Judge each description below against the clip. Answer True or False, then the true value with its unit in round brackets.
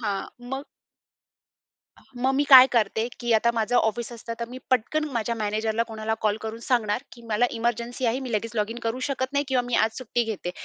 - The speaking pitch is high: True (235 Hz)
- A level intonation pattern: True (2.3 semitones)